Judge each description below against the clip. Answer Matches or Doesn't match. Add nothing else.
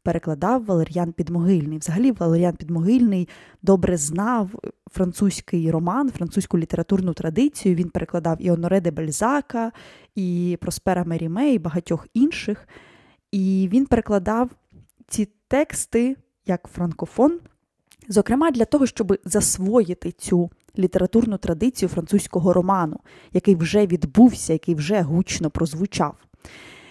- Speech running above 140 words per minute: Doesn't match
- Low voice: Doesn't match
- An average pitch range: Matches